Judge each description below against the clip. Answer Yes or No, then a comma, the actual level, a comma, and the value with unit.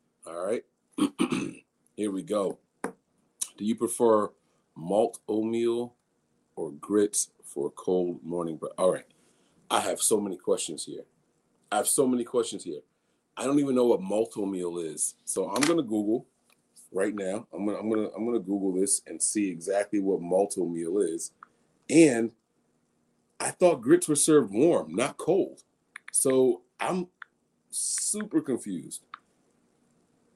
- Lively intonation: Yes, wide, 8.5 semitones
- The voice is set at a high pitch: No, low, 115 Hz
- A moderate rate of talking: Yes, average, 150 wpm